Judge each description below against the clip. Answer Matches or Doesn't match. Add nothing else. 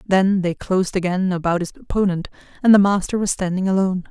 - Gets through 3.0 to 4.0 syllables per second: Doesn't match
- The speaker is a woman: Matches